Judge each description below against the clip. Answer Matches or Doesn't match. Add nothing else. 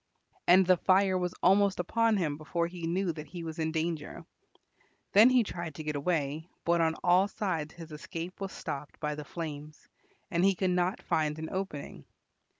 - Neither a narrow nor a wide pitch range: Matches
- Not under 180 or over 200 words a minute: Matches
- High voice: Doesn't match